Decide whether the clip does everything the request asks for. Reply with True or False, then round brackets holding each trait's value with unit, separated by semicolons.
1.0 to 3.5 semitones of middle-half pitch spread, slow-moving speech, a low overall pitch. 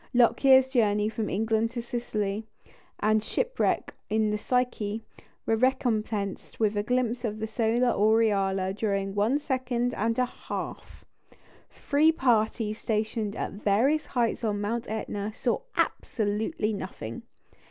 False (2.7 semitones; 130 wpm; 220 Hz)